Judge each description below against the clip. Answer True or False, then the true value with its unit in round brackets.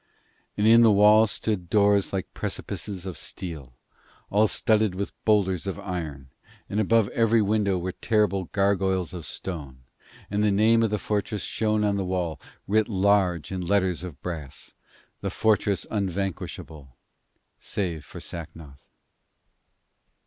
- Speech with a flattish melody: False (3.3 semitones)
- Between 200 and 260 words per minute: False (140 wpm)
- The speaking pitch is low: True (95 Hz)